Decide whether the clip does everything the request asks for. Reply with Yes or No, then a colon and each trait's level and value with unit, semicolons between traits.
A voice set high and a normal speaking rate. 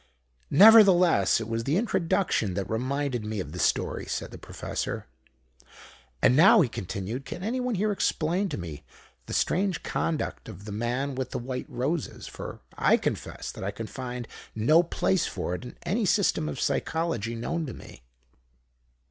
No: low, 135 Hz; average, 165 wpm